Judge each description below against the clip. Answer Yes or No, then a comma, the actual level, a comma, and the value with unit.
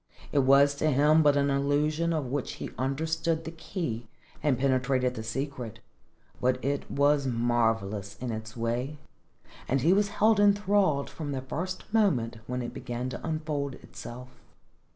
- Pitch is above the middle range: No, medium, 140 Hz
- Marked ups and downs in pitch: No, average, 4.1 semitones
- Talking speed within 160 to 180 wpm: No, average, 150 wpm